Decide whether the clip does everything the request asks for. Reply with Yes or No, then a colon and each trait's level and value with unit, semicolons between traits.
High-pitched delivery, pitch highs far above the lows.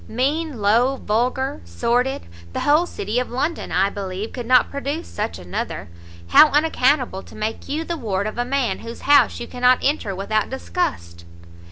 No: very high, 250 Hz; average, 4.9 semitones